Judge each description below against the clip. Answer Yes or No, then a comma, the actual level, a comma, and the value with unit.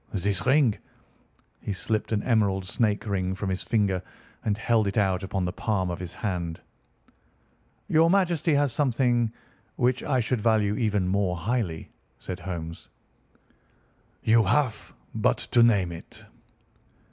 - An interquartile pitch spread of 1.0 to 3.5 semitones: No, average, 4.3 semitones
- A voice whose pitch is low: Yes, low, 105 Hz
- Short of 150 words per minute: Yes, average, 140 wpm